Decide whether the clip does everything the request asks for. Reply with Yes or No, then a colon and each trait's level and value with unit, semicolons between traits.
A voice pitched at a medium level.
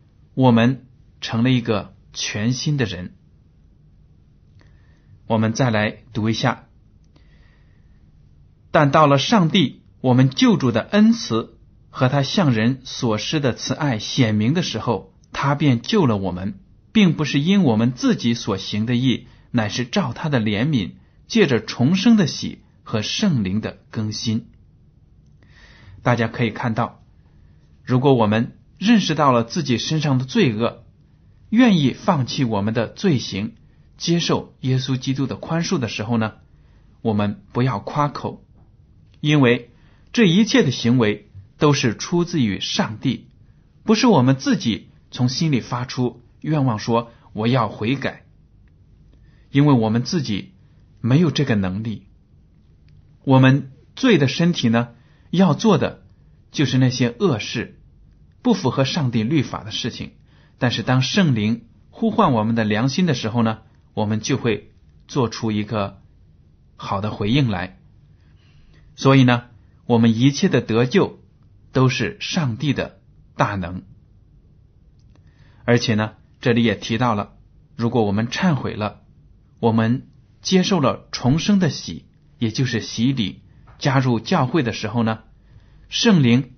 No: low, 120 Hz